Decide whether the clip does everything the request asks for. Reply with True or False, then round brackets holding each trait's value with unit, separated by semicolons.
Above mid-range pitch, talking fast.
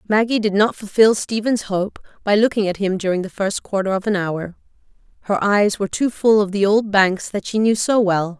True (205 Hz; 220 wpm)